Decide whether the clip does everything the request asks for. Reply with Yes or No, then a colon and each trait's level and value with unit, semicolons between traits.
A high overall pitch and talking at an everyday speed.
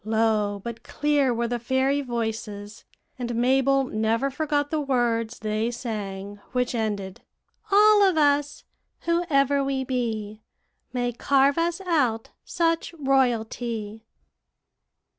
No: high, 245 Hz; slow, 115 wpm